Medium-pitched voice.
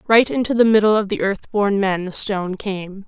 No: high, 200 Hz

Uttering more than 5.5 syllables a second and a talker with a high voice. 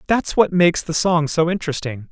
No: 5.7 syllables/s; medium, 170 Hz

